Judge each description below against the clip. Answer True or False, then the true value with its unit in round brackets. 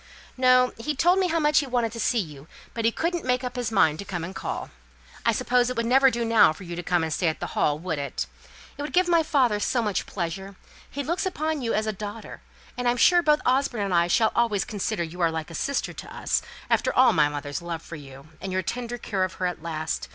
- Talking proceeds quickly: True (260 wpm)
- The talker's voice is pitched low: False (220 Hz)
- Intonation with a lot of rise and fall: True (6.8 semitones)